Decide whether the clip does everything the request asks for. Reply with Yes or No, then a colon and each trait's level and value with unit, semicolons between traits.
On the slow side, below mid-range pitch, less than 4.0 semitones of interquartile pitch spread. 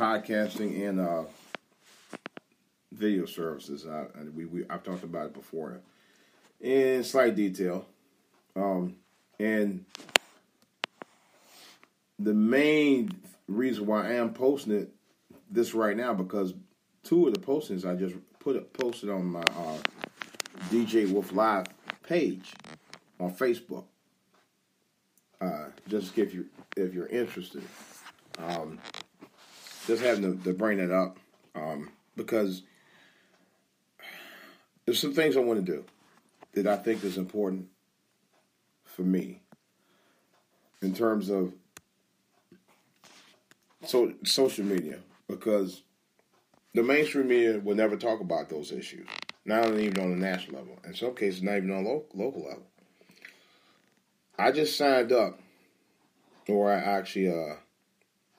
Yes: slow, 120 wpm; low, 100 Hz; average, 3.4 semitones